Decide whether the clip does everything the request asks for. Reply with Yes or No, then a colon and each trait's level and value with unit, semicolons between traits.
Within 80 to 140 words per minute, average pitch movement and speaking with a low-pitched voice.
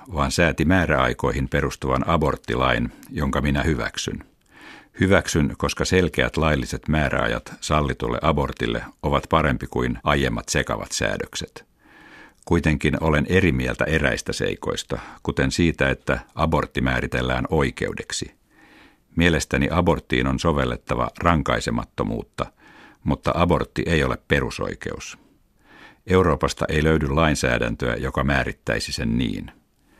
Yes: average, 100 wpm; average, 3.6 semitones; very low, 70 Hz